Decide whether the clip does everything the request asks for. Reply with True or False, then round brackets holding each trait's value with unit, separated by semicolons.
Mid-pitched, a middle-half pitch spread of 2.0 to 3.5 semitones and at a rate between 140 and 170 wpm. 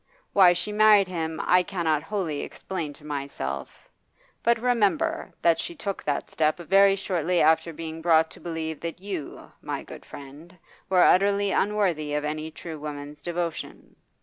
False (170 Hz; 4.2 semitones; 155 wpm)